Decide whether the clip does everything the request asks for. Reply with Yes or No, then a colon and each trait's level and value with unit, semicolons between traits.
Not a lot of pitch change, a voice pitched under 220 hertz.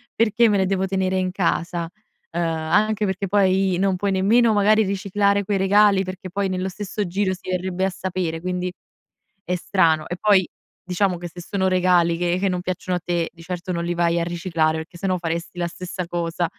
Yes: narrow, 2.1 semitones; medium, 185 Hz